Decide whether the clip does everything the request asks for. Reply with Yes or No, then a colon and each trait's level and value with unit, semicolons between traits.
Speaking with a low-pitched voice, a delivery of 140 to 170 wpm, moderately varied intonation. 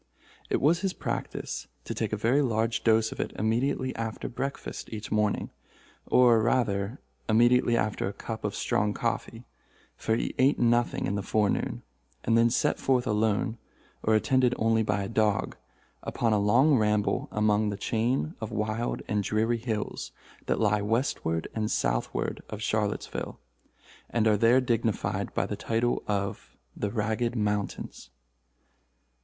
No: low, 110 Hz; average, 150 wpm; narrow, 2.2 semitones